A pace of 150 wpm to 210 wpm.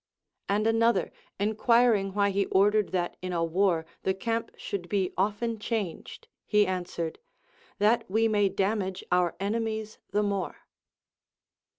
No: slow, 135 wpm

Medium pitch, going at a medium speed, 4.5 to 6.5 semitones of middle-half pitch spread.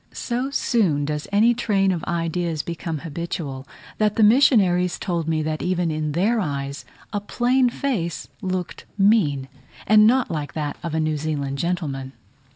Yes: medium, 170 Hz; average, 160 wpm; wide, 5.5 semitones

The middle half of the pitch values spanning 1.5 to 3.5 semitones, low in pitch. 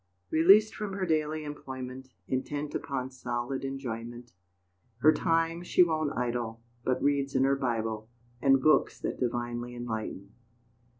No: average, 4.3 semitones; low, 130 Hz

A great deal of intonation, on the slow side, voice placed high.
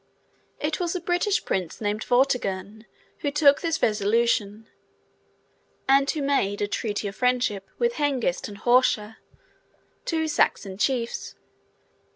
Yes: wide, 5.7 semitones; slow, 125 wpm; high, 240 Hz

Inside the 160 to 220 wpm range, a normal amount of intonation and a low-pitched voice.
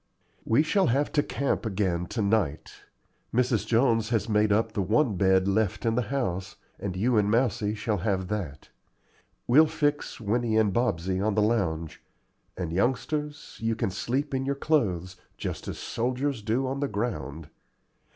Yes: average, 165 wpm; average, 4.5 semitones; low, 110 Hz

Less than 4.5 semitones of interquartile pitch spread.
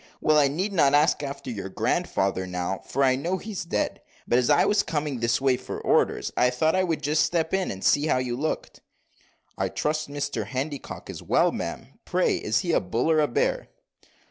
Yes: average, 4.1 semitones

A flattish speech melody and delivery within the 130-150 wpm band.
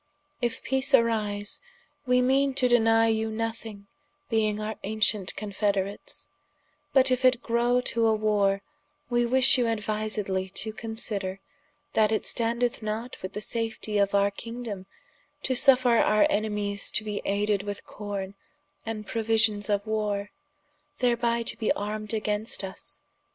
Yes: narrow, 2.3 semitones; average, 140 wpm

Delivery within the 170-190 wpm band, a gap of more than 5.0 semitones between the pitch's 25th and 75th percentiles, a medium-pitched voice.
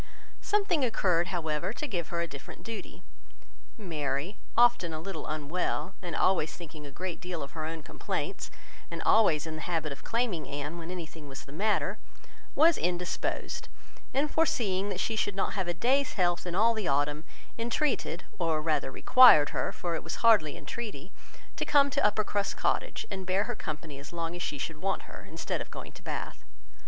Yes: average, 185 wpm; wide, 5.4 semitones; medium, 175 Hz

